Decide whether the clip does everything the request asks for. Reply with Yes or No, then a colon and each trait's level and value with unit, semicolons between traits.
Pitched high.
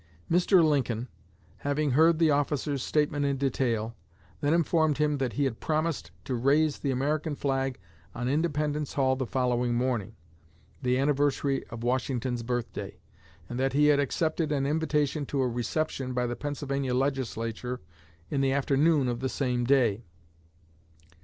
No: low, 135 Hz